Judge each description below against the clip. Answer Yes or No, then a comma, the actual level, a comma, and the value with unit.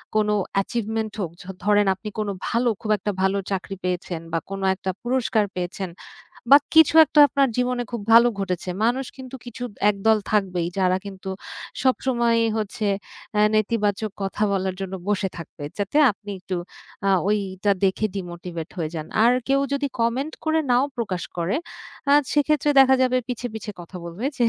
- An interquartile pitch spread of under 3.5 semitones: No, average, 4.3 semitones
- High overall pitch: Yes, high, 210 Hz